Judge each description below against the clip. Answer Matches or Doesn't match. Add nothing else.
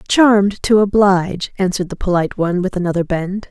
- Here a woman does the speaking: Matches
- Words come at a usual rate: Matches